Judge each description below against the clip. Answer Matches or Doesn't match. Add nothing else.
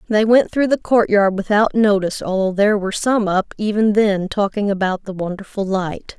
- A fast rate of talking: Doesn't match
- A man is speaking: Doesn't match